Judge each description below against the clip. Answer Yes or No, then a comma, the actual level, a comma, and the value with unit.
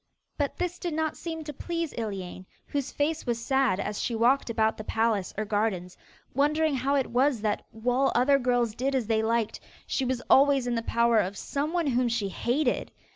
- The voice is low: No, high, 245 Hz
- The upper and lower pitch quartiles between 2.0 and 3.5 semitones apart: No, average, 4.2 semitones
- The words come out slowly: No, average, 195 wpm